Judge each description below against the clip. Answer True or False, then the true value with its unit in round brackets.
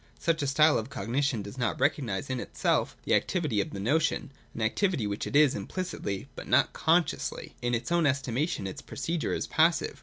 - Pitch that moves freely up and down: True (5.9 semitones)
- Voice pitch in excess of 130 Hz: True (140 Hz)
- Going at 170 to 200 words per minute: True (195 wpm)